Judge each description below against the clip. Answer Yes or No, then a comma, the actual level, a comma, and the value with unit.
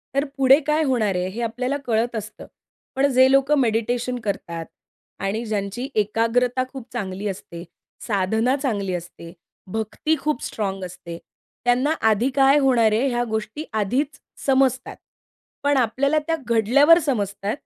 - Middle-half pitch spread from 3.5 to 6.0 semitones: Yes, average, 4.6 semitones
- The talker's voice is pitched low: No, high, 235 Hz